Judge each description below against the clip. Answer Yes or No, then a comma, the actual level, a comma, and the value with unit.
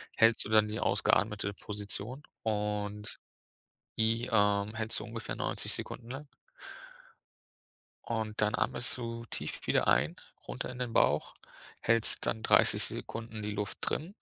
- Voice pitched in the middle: No, low, 110 Hz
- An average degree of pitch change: No, narrow, 1.9 semitones